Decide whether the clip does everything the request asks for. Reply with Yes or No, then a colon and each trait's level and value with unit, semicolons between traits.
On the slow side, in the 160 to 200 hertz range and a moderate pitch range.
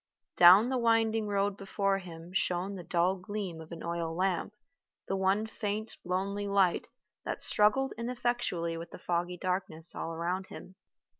No: average, 155 wpm; high, 190 Hz; average, 3.1 semitones